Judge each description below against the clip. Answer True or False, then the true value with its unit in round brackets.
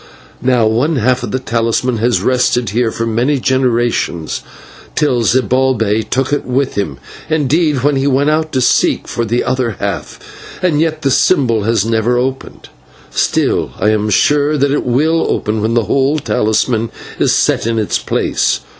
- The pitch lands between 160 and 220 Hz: False (125 Hz)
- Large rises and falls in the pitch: False (3.5 semitones)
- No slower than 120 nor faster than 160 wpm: False (170 wpm)